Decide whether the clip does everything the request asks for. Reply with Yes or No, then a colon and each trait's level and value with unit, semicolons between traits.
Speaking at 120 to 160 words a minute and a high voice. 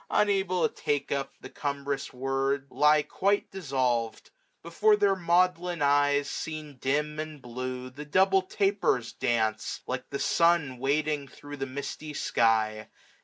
No: average, 140 wpm; medium, 145 Hz